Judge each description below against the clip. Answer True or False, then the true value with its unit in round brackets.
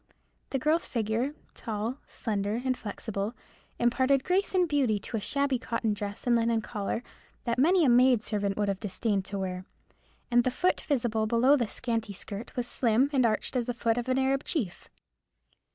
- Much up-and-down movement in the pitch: False (3.6 semitones)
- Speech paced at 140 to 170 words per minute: False (185 wpm)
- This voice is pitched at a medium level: False (235 Hz)